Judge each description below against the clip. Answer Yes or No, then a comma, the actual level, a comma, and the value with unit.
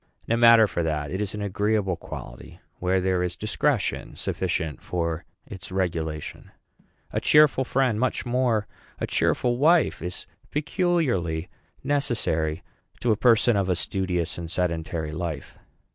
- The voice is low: Yes, very low, 95 Hz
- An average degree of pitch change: No, wide, 6.2 semitones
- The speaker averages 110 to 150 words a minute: Yes, average, 140 wpm